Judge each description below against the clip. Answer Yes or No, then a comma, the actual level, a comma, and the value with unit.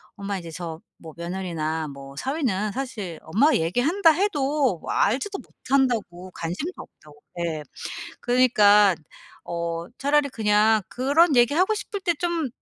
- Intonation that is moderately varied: No, wide, 8.8 semitones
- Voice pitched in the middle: No, high, 215 Hz